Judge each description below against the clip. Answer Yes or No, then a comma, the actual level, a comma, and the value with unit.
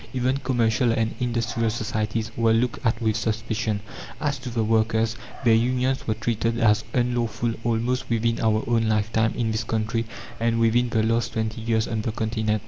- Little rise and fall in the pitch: Yes, narrow, 1.1 semitones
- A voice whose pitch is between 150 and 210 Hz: No, low, 115 Hz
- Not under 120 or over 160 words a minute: No, average, 175 wpm